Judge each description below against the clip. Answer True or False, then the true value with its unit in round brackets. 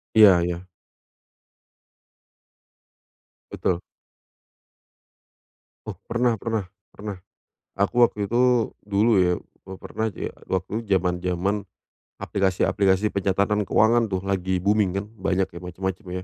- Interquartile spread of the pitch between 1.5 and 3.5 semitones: True (2.6 semitones)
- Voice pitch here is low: True (100 Hz)